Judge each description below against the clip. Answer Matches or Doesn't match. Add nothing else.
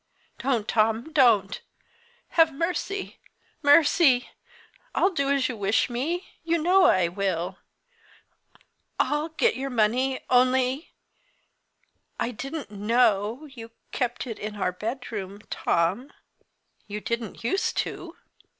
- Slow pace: Matches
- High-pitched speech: Matches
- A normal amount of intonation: Doesn't match